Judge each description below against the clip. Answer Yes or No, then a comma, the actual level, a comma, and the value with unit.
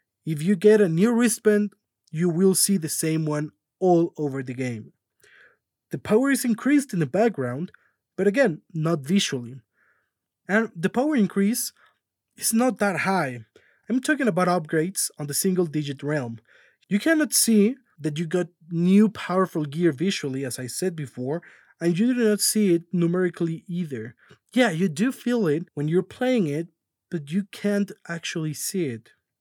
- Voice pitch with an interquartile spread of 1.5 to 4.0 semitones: No, average, 5.3 semitones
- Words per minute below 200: Yes, average, 165 wpm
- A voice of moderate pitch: Yes, medium, 180 Hz